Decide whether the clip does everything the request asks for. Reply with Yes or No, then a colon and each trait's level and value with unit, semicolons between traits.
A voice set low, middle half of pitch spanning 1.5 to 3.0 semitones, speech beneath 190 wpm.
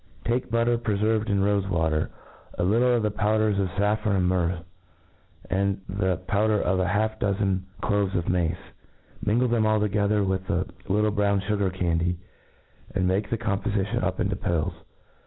Yes: low, 100 Hz; narrow, 2.5 semitones; average, 170 wpm